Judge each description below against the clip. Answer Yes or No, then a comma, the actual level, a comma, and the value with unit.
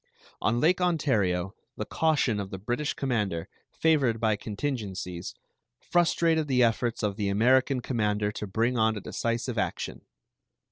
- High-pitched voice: No, low, 115 Hz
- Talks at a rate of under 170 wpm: Yes, average, 140 wpm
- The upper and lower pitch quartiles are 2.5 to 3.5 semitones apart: No, average, 4.7 semitones